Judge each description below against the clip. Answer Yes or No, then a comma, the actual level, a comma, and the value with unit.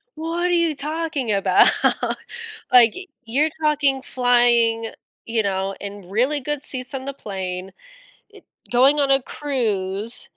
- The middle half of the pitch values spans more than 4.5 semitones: Yes, average, 5.2 semitones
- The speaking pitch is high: Yes, very high, 250 Hz